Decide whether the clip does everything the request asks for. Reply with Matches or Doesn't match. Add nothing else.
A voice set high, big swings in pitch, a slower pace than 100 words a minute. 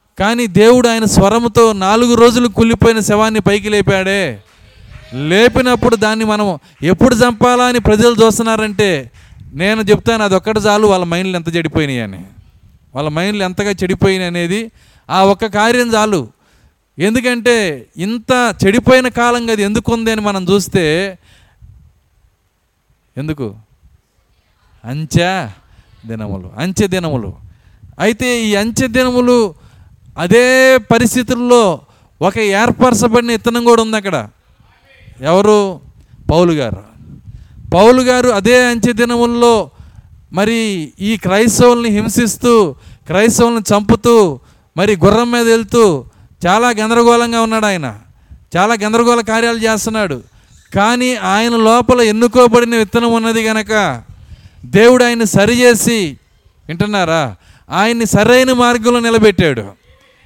Doesn't match